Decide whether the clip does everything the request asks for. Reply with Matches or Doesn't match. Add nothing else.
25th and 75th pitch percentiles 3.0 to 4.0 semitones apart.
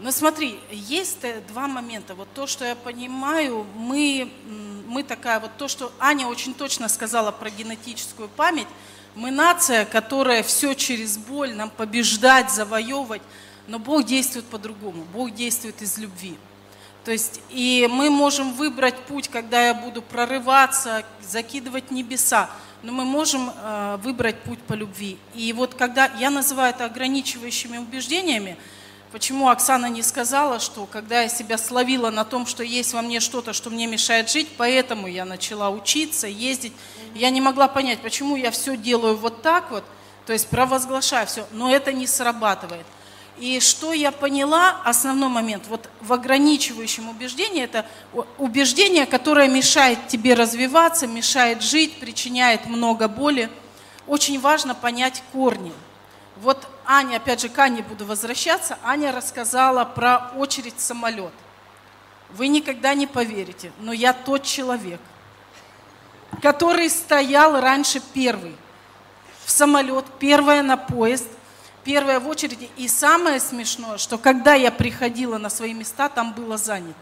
Matches